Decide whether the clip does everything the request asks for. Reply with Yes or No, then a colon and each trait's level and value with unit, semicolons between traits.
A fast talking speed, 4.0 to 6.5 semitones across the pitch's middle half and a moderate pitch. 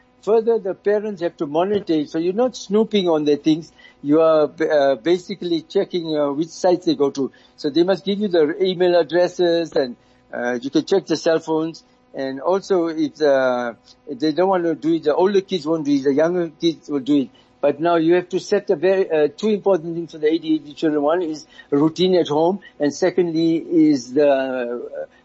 Yes: fast, 210 wpm; average, 4.3 semitones; medium, 165 Hz